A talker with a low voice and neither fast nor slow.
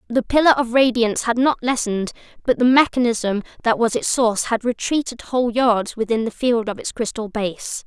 No: high, 235 Hz; average, 185 wpm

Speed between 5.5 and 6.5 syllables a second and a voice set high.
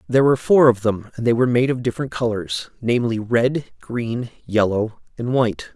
No: 5.6 syllables/s; low, 120 Hz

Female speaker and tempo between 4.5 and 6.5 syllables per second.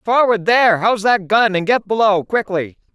Yes: female; 5.2 syllables/s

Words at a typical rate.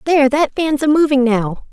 No: fast, 210 wpm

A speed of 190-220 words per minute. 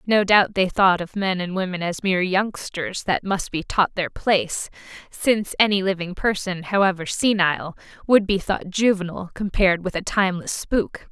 No: average, 175 wpm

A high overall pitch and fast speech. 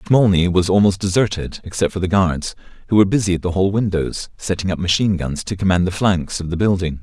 No: very low, 95 Hz; fast, 220 wpm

